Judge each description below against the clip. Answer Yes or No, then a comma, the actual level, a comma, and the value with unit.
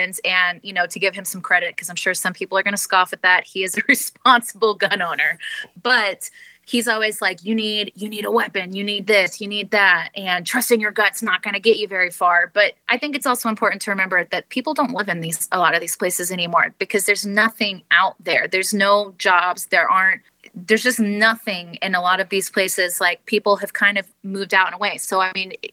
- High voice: Yes, high, 200 Hz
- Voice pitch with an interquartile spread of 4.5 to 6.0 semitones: No, average, 2.8 semitones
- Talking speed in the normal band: No, fast, 245 wpm